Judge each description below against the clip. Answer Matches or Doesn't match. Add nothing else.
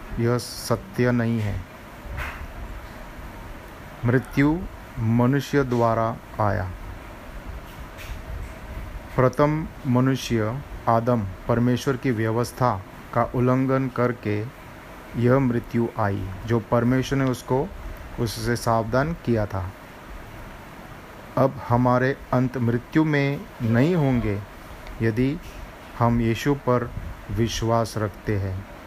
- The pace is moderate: Doesn't match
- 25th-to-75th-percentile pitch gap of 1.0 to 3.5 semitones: Matches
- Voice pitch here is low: Matches